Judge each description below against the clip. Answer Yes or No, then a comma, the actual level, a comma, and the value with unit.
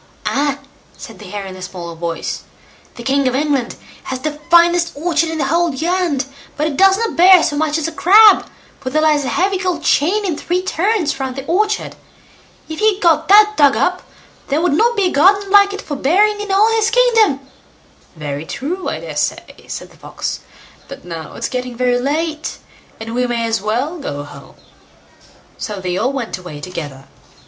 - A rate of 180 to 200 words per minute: Yes, average, 195 wpm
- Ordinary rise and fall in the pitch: No, wide, 6.9 semitones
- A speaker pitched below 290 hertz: No, very high, 305 Hz